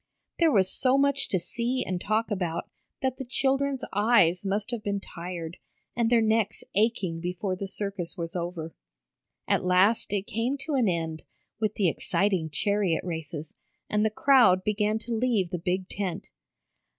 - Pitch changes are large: No, average, 4.3 semitones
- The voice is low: No, high, 200 Hz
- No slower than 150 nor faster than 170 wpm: Yes, average, 165 wpm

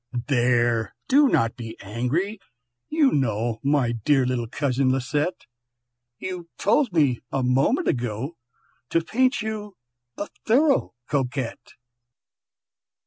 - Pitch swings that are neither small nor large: No, wide, 8.7 semitones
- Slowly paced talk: Yes, slow, 110 wpm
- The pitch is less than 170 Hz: Yes, low, 135 Hz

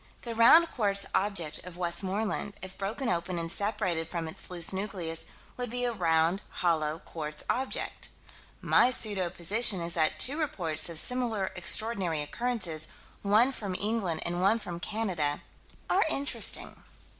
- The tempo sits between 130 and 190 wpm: Yes, average, 145 wpm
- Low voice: No, high, 190 Hz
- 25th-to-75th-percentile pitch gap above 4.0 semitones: Yes, average, 5.0 semitones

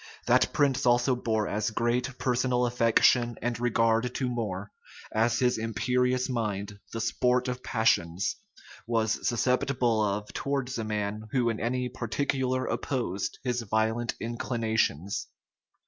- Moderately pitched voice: No, low, 120 Hz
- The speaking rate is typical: No, slow, 130 wpm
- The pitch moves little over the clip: Yes, narrow, 2.3 semitones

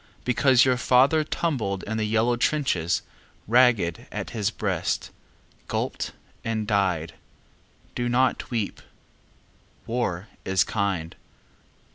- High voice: No, low, 110 Hz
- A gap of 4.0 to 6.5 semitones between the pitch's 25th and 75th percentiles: Yes, average, 4.3 semitones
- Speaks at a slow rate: Yes, slow, 105 wpm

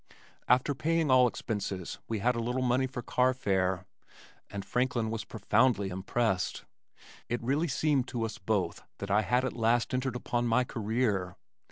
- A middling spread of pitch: Yes, average, 3.8 semitones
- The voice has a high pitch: No, low, 120 Hz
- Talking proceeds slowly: No, average, 160 wpm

